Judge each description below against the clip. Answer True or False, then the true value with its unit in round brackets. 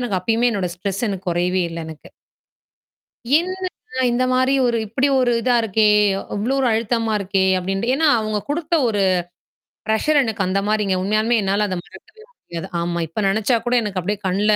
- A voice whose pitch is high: True (215 Hz)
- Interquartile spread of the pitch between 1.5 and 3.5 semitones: False (4.0 semitones)